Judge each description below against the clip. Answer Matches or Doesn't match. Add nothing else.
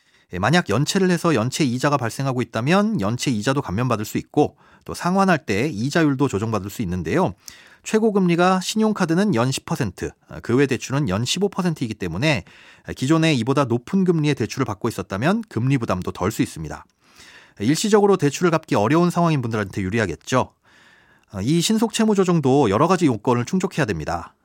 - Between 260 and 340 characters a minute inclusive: Doesn't match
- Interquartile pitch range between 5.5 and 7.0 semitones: Doesn't match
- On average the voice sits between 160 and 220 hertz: Doesn't match